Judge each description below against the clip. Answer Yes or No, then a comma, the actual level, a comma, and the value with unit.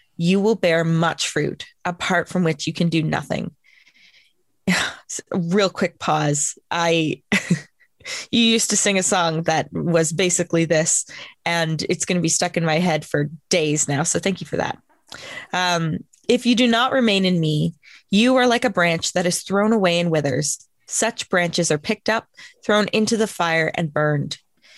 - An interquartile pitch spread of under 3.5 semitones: No, average, 3.9 semitones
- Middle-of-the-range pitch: Yes, medium, 175 Hz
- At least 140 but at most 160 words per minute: No, average, 175 wpm